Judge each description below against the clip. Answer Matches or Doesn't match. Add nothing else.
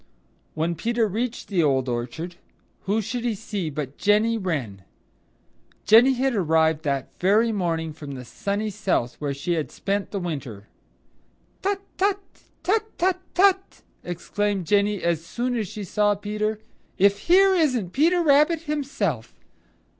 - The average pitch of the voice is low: Doesn't match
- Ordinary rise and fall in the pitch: Doesn't match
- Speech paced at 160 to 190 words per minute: Doesn't match